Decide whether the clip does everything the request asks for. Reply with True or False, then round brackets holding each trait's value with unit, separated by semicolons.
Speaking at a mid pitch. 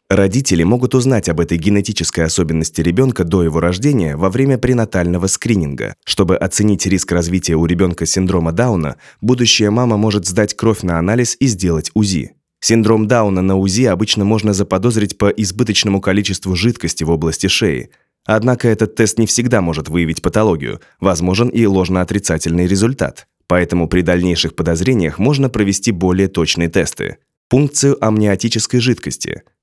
False (100 Hz)